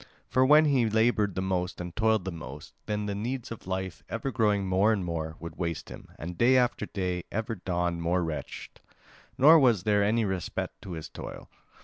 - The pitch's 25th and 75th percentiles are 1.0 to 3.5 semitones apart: No, average, 4.3 semitones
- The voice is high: No, low, 100 Hz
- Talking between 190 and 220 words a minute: Yes, average, 200 wpm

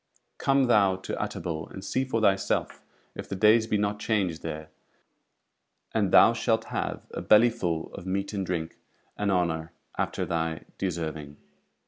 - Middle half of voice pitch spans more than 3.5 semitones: Yes, average, 4.7 semitones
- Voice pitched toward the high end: No, very low, 95 Hz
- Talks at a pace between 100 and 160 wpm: Yes, average, 155 wpm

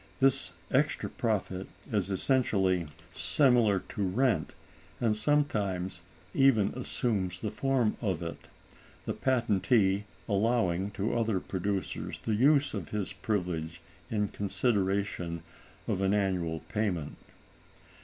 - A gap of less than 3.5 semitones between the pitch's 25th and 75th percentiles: No, average, 4.1 semitones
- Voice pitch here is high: No, low, 100 Hz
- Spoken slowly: Yes, slow, 110 wpm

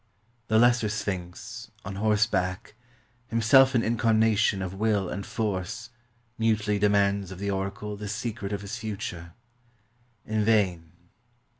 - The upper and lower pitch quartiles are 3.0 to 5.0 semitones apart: No, narrow, 2.4 semitones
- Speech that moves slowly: Yes, slow, 125 wpm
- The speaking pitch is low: Yes, low, 105 Hz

